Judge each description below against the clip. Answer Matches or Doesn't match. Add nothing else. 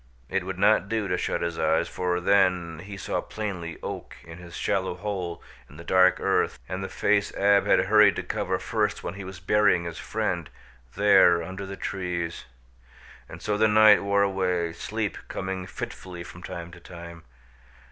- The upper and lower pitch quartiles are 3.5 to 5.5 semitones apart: Doesn't match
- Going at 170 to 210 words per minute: Matches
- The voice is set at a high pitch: Doesn't match